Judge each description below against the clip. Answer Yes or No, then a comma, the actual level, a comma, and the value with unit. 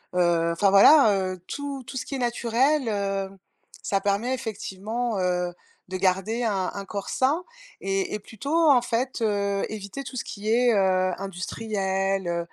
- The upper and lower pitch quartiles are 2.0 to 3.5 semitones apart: No, average, 3.9 semitones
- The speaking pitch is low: No, high, 205 Hz